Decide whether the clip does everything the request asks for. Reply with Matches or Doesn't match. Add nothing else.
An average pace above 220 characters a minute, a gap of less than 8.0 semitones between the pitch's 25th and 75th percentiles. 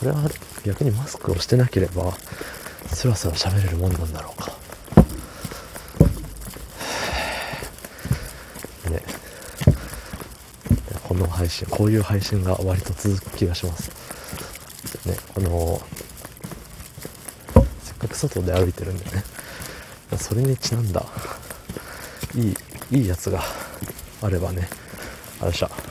Doesn't match